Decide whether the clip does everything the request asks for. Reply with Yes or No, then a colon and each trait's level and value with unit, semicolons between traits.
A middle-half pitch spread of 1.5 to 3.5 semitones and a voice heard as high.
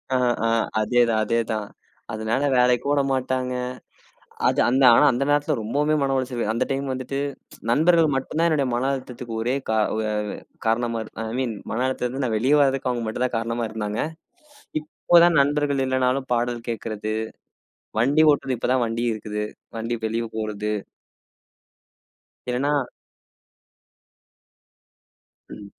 No: average, 3.1 semitones; low, 125 Hz